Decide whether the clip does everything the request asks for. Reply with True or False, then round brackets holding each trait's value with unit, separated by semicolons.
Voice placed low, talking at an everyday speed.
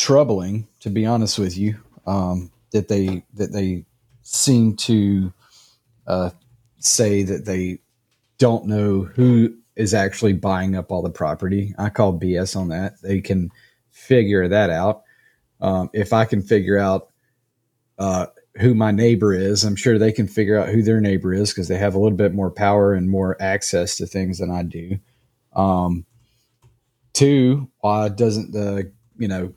True (105 Hz; 165 wpm)